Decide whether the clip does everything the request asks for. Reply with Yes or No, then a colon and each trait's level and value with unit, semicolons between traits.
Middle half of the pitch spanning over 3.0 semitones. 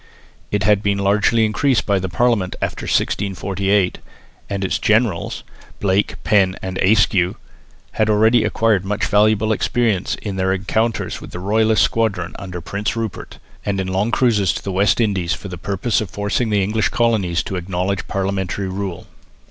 No: narrow, 2.4 semitones